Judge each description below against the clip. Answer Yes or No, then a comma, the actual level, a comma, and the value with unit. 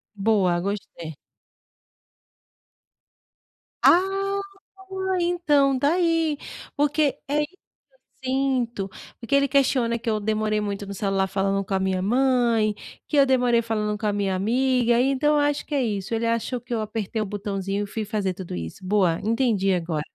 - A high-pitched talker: Yes, high, 225 Hz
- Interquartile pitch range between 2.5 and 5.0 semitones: No, wide, 5.6 semitones